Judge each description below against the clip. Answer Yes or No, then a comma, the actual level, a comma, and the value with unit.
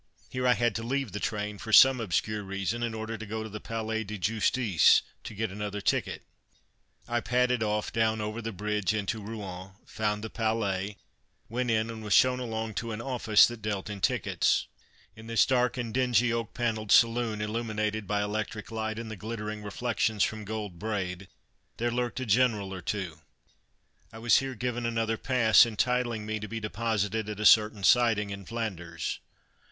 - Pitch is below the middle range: Yes, low, 110 Hz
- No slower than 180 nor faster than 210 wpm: Yes, average, 185 wpm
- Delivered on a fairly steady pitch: Yes, narrow, 1.9 semitones